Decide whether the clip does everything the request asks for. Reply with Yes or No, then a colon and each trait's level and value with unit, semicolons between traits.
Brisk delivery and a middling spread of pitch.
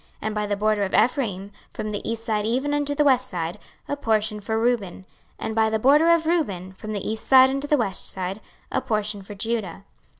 Yes: fast, 230 wpm; average, 4.3 semitones